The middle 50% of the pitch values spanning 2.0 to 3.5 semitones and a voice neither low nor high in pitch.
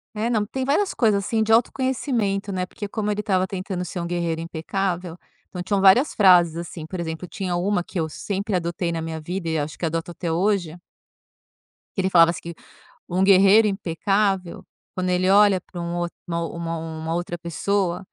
Yes: average, 2.9 semitones; medium, 180 Hz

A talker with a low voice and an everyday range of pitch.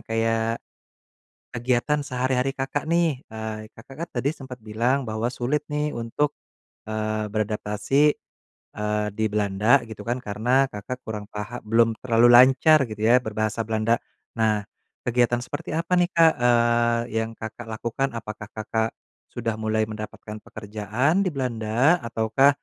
Yes: low, 115 Hz; average, 3.4 semitones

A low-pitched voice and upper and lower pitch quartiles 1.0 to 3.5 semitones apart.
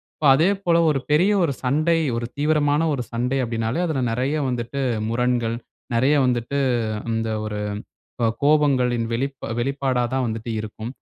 No: low, 130 Hz; average, 3.9 semitones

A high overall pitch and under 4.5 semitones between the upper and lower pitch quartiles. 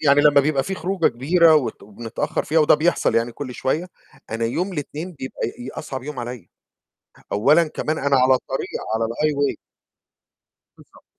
No: medium, 140 Hz; average, 4.0 semitones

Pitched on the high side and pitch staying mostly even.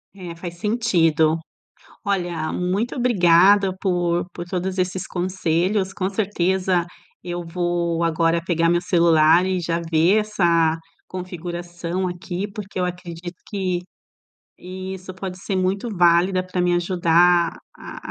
No: medium, 180 Hz; narrow, 1.7 semitones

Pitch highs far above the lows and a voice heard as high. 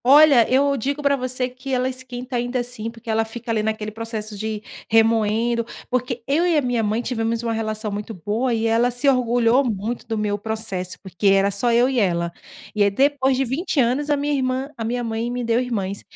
No: average, 2.8 semitones; high, 235 Hz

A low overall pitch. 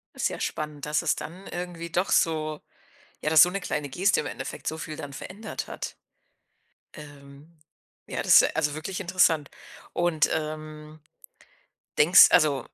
No: medium, 155 Hz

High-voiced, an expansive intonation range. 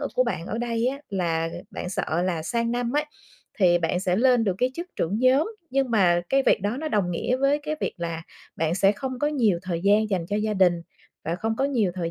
Yes: high, 210 Hz; wide, 6.4 semitones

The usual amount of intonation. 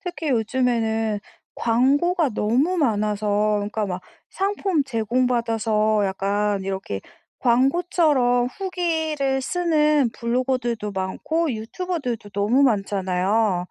No: wide, 5.8 semitones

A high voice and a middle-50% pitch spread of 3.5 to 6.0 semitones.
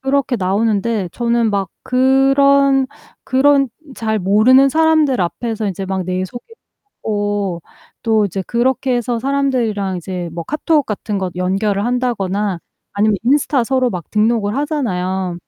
Yes: high, 225 Hz; average, 5.3 semitones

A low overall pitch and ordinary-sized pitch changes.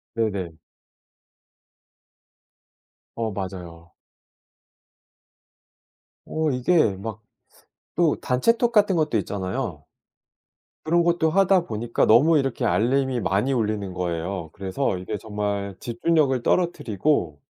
No: low, 115 Hz; wide, 7.8 semitones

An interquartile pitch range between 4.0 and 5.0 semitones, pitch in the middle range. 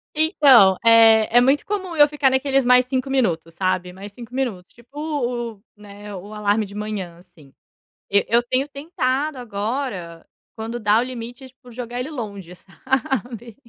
No: average, 4.6 semitones; high, 235 Hz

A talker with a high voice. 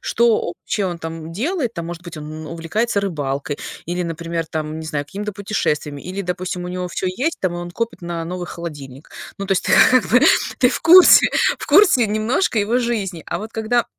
No: medium, 180 Hz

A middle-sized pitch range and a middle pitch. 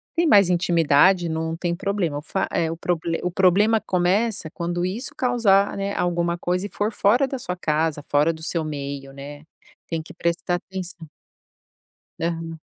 Yes: average, 3.3 semitones; medium, 175 Hz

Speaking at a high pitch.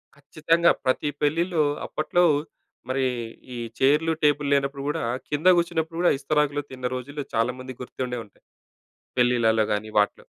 No: medium, 140 Hz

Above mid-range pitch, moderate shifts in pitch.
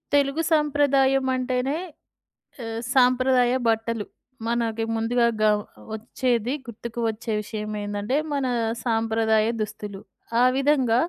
Yes: high, 235 Hz; average, 3.0 semitones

